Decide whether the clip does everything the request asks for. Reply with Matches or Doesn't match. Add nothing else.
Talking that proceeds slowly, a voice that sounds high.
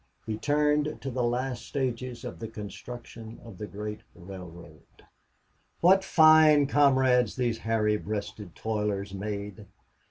Doesn't match